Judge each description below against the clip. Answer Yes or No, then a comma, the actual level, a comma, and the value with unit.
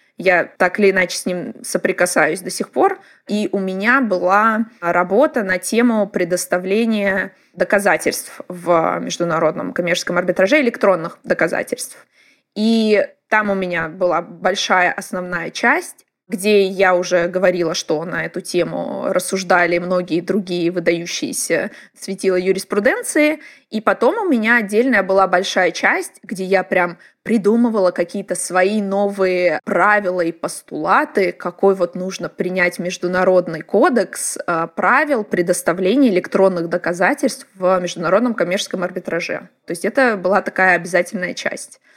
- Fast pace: No, average, 125 wpm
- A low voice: No, high, 190 Hz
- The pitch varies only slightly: No, average, 3.3 semitones